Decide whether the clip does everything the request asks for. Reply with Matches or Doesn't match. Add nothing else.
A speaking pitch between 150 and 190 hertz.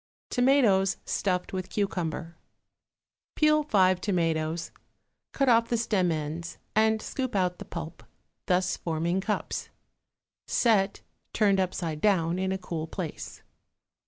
Matches